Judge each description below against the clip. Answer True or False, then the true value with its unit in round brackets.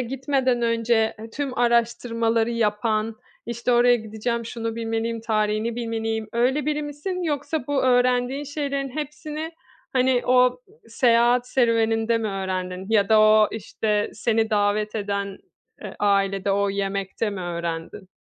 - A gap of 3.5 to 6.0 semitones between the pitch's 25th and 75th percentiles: False (2.8 semitones)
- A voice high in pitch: True (230 Hz)